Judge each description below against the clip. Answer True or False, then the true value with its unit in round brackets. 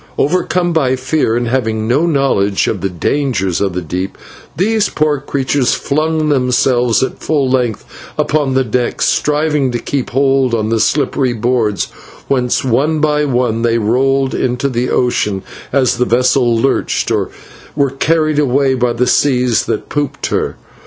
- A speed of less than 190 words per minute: True (160 wpm)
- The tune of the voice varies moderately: True (3.3 semitones)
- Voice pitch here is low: True (130 Hz)